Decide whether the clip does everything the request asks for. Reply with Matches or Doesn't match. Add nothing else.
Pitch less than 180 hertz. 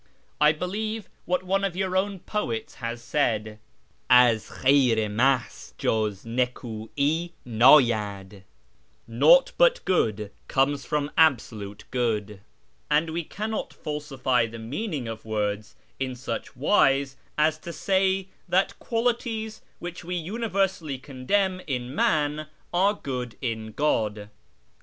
Matches